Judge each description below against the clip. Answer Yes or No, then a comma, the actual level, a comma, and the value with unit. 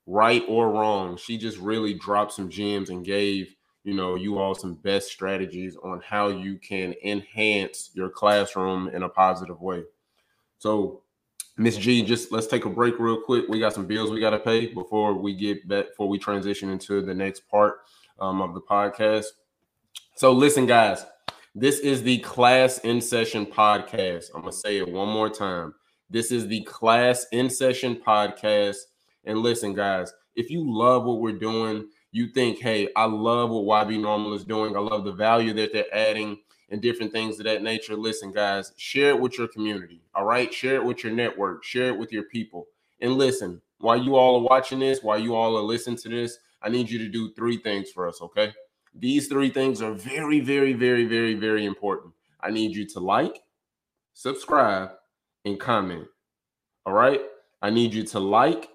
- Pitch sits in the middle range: No, low, 110 Hz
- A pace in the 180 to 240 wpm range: Yes, average, 190 wpm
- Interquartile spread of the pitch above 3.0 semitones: No, average, 2.7 semitones